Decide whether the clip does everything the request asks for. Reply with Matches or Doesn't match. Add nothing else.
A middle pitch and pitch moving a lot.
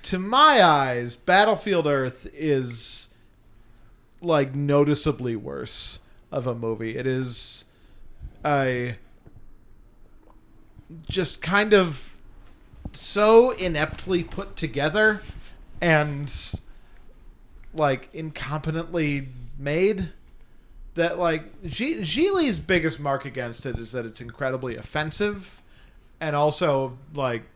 Matches